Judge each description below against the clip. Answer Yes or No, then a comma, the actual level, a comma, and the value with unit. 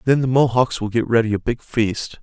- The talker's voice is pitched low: Yes, low, 120 Hz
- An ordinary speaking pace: No, fast, 245 wpm